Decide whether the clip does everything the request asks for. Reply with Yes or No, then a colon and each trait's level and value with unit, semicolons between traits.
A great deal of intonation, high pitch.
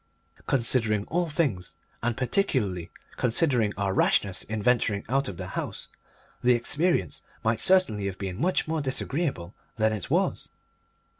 No: wide, 5.8 semitones; low, 115 Hz